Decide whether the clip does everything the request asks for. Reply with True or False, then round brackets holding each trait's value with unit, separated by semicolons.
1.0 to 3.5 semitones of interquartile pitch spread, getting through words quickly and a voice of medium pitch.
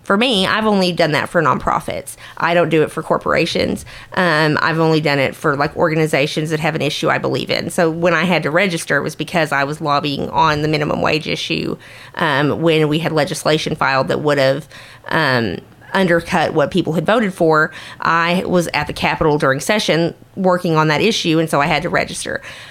True (2.6 semitones; 210 wpm; 160 Hz)